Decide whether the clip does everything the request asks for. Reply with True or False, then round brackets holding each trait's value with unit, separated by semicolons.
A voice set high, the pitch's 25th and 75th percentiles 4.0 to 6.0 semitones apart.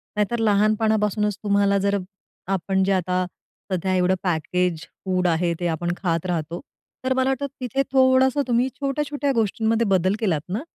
True (200 Hz; 4.6 semitones)